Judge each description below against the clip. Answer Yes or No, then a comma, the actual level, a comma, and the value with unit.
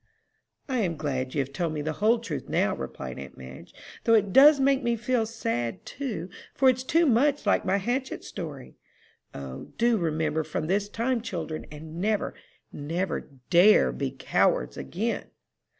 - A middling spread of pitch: No, wide, 8.1 semitones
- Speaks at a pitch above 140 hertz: Yes, medium, 185 Hz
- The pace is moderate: Yes, average, 165 wpm